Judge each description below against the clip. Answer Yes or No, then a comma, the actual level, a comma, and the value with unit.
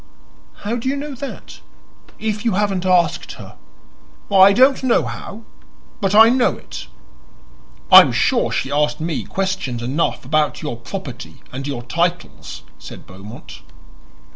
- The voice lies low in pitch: No, medium, 180 Hz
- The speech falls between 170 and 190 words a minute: No, average, 140 wpm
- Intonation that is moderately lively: No, wide, 7.8 semitones